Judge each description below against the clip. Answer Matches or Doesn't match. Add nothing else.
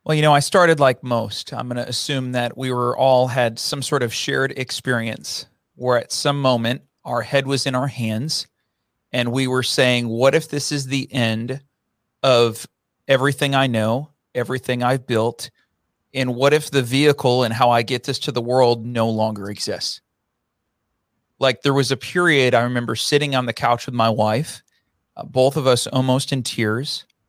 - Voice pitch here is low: Matches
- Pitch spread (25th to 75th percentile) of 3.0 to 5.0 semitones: Doesn't match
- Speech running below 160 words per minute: Doesn't match